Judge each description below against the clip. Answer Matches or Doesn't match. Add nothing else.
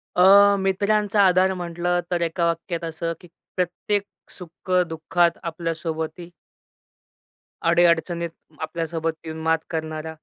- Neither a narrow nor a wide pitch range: Doesn't match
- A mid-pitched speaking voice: Matches